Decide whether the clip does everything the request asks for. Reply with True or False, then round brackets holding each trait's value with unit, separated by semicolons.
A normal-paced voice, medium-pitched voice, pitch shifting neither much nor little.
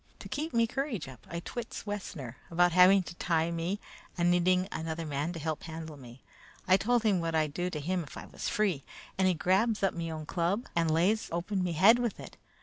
False (225 wpm; 175 Hz; 3.5 semitones)